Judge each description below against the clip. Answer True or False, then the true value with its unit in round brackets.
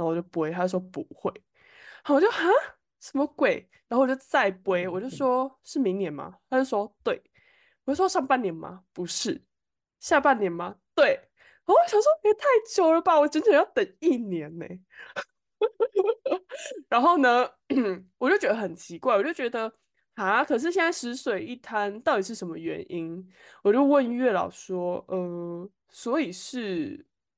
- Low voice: False (260 Hz)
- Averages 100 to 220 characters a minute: False (240 characters per minute)